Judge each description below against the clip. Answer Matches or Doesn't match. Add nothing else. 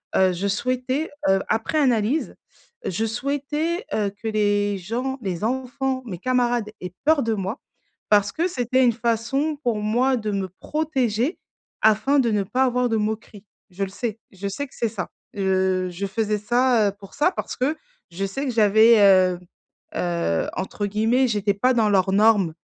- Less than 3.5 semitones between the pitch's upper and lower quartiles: Doesn't match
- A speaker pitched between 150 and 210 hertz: Doesn't match